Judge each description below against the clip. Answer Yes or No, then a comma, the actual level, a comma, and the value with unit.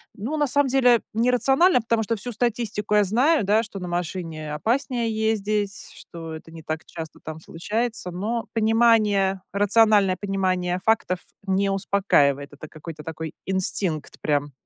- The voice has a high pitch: Yes, high, 200 Hz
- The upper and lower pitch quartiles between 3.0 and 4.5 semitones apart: No, average, 4.9 semitones